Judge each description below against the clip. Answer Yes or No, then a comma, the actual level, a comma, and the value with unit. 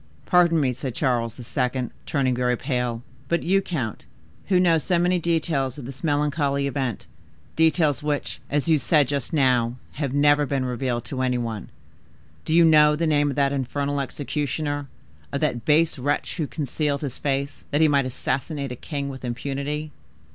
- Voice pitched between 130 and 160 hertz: Yes, medium, 140 Hz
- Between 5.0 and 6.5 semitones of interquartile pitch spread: No, average, 2.9 semitones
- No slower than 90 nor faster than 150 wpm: No, average, 170 wpm